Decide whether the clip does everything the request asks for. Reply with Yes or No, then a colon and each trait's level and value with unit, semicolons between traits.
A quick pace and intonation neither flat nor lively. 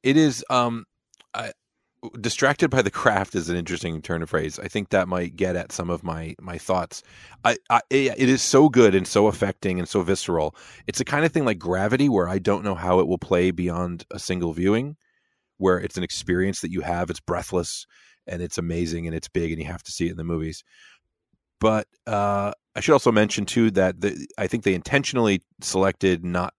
Yes: fast, 215 wpm; average, 3.1 semitones